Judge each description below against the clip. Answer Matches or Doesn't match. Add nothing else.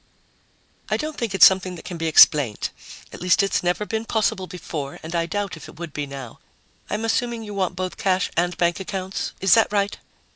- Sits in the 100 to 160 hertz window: Doesn't match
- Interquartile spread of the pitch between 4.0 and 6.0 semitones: Doesn't match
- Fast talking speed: Matches